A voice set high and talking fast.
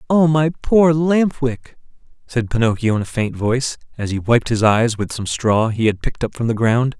No: low, 125 Hz; fast, 225 wpm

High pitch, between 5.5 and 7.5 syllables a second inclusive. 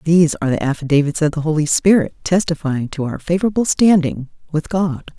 No: medium, 160 Hz; 5.9 syllables/s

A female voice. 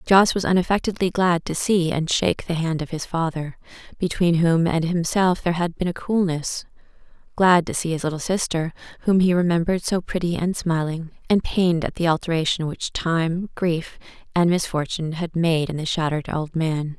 Yes: female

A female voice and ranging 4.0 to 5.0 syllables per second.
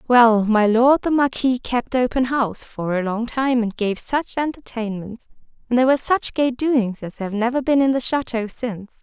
Yes: female; 4.9 syllables/s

